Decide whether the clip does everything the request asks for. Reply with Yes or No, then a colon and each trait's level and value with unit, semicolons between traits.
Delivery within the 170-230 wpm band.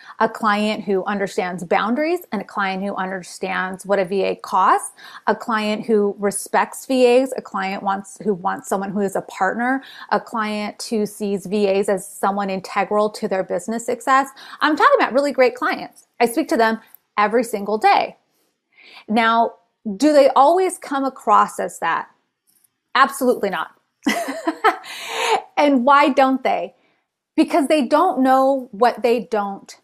No: average, 150 wpm